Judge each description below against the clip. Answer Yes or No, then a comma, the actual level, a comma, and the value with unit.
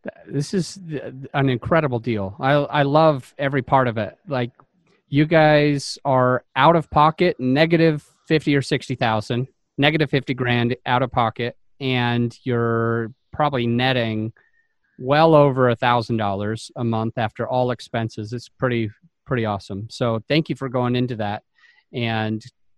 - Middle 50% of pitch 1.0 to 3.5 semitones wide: No, average, 4.0 semitones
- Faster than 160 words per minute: No, average, 155 wpm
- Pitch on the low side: Yes, low, 125 Hz